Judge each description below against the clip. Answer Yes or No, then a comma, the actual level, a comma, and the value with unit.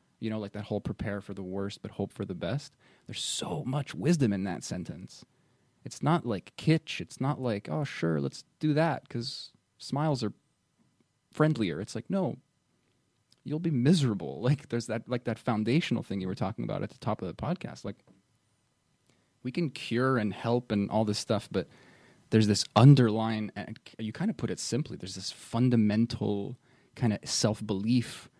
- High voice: No, low, 115 Hz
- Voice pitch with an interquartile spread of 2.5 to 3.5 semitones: No, average, 4.1 semitones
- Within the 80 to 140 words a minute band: No, average, 185 wpm